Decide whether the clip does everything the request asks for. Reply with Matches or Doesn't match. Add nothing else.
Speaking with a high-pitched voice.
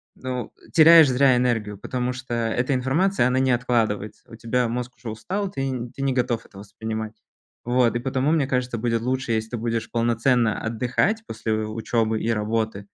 Doesn't match